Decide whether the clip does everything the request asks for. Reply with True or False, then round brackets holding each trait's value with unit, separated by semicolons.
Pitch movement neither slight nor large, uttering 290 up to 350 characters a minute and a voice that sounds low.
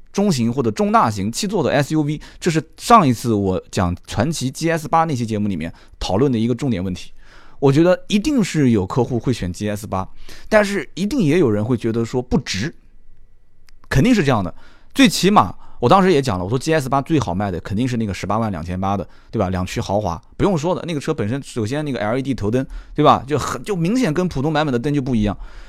False (7.5 semitones; 340 characters per minute; 125 Hz)